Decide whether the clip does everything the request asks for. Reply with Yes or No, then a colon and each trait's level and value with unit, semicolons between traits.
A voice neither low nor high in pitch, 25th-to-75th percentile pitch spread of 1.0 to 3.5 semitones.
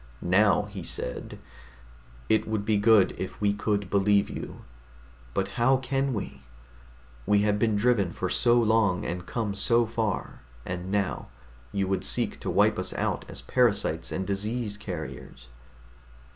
No: low, 105 Hz; average, 2.7 semitones